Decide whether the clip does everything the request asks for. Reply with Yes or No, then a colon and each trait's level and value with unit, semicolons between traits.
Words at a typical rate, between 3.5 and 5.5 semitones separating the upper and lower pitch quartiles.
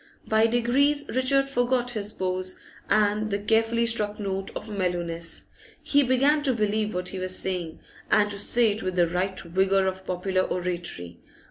Yes: average, 165 wpm; average, 4.0 semitones